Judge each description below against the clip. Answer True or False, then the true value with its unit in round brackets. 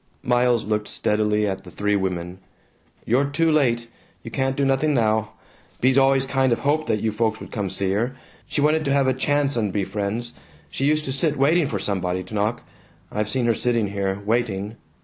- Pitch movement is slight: False (4.7 semitones)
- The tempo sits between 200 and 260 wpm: True (205 wpm)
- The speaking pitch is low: True (115 Hz)